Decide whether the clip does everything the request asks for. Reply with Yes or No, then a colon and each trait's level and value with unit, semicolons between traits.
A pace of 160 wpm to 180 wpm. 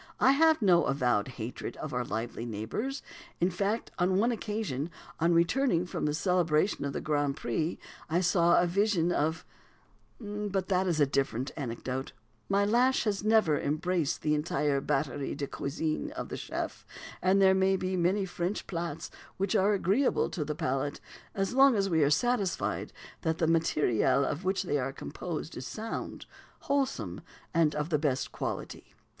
Yes: average, 165 wpm